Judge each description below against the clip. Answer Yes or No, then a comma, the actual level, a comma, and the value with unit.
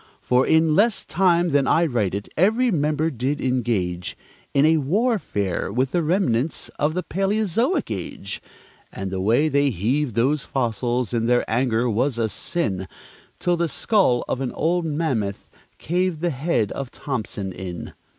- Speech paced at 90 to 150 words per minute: No, average, 160 wpm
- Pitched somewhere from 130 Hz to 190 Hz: Yes, medium, 140 Hz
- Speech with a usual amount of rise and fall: No, wide, 6.8 semitones